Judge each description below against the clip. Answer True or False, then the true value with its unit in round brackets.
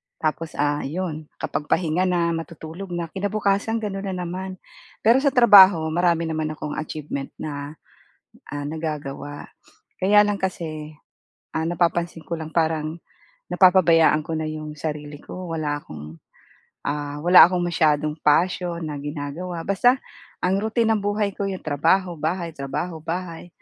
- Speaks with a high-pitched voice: False (165 Hz)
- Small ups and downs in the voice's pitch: False (3.4 semitones)